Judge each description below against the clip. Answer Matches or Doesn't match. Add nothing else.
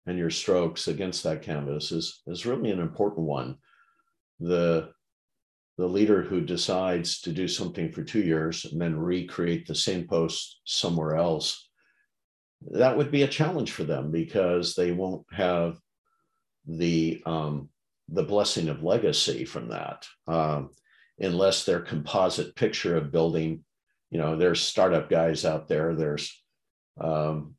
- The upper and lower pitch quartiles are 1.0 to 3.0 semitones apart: Matches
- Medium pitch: Doesn't match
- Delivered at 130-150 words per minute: Matches